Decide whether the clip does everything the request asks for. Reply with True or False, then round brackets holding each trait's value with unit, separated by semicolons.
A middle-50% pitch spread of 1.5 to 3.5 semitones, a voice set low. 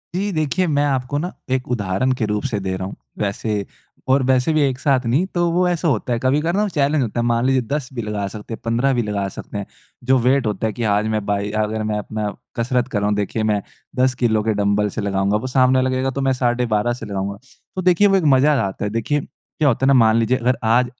False (4.3 semitones; 120 Hz)